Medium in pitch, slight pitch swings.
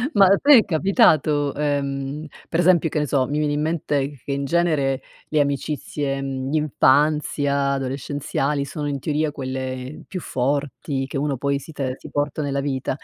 Yes: medium, 145 Hz; narrow, 1.8 semitones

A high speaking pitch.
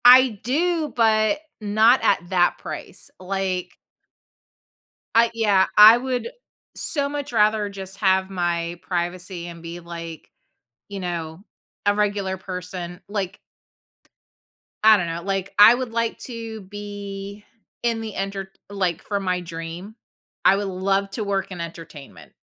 Yes: high, 195 Hz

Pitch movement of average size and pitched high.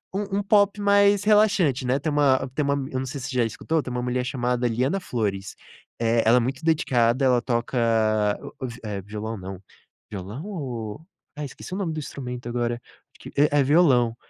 No: average, 4.9 semitones; low, 130 Hz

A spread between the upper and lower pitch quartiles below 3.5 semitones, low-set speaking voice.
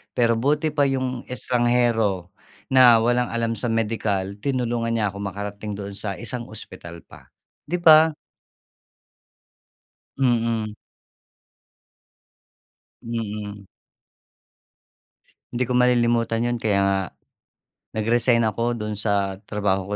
Yes: average, 3.0 semitones; low, 115 Hz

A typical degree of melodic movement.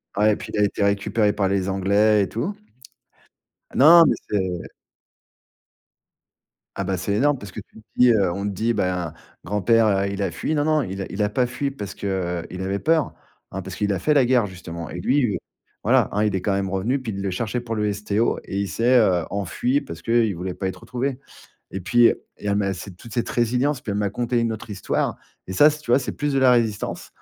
Yes: average, 3.9 semitones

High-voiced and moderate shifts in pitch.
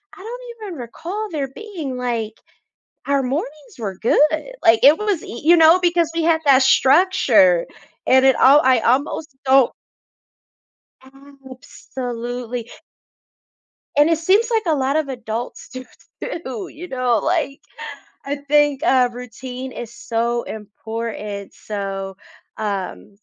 Yes: very high, 265 Hz; average, 4.9 semitones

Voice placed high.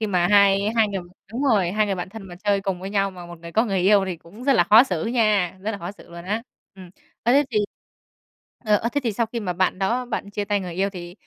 Yes: high, 200 Hz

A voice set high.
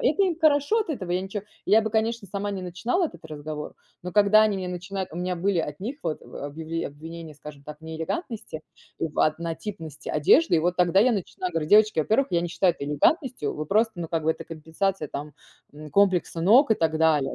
No: medium, 180 Hz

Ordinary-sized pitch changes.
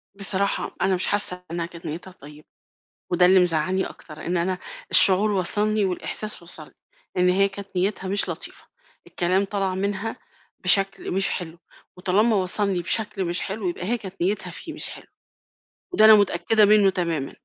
No: narrow, 2.2 semitones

